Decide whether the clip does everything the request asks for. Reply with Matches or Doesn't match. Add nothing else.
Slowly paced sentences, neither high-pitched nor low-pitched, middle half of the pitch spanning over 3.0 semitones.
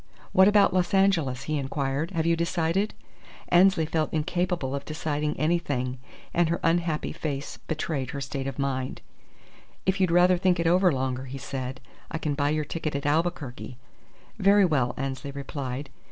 Doesn't match